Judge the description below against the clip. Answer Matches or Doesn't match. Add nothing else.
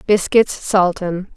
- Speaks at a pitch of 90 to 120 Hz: Doesn't match